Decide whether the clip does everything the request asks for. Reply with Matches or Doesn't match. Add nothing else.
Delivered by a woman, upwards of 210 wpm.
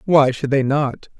Doesn't match